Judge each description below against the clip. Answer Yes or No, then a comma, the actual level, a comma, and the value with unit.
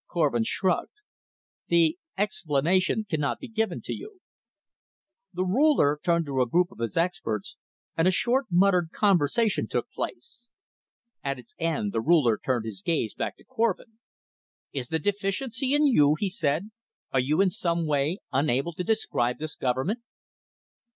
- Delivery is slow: No, average, 150 wpm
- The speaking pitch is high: No, medium, 170 Hz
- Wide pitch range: Yes, wide, 6.3 semitones